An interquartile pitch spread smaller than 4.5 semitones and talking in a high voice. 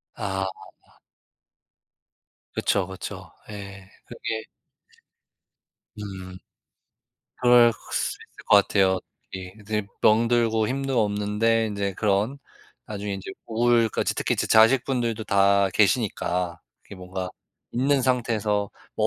No: average, 2.9 semitones; low, 105 Hz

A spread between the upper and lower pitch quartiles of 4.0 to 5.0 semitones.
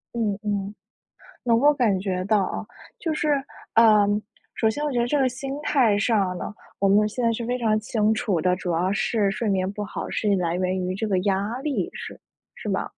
No: average, 3.5 semitones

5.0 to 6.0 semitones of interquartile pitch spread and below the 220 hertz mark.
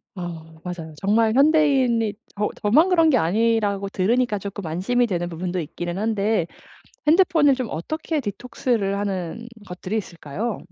Yes: wide, 5.5 semitones; high, 210 Hz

